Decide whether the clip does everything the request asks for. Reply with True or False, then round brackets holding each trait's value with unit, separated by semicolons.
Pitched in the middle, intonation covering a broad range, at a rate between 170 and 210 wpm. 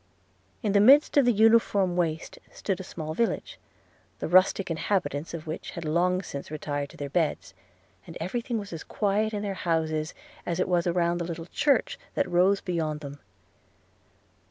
False (175 Hz; 4.0 semitones; 180 wpm)